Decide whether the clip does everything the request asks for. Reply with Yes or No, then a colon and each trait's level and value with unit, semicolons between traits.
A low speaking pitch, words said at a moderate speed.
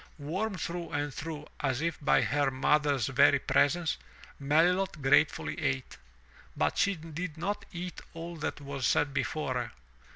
No: medium, 150 Hz; average, 150 wpm